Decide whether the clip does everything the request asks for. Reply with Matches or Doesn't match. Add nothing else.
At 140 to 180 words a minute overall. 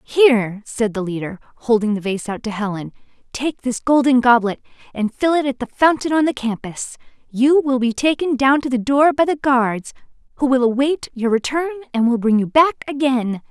Doesn't match